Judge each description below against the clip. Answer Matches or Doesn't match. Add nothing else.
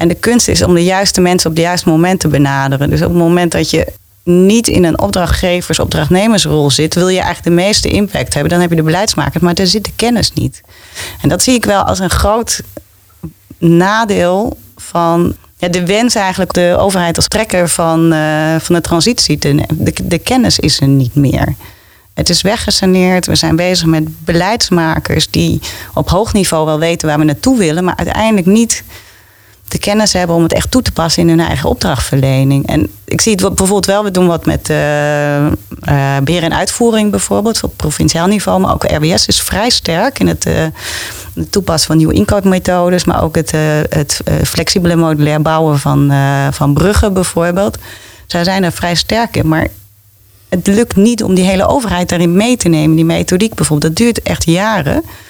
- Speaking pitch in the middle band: Matches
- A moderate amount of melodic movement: Matches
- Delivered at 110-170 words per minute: Doesn't match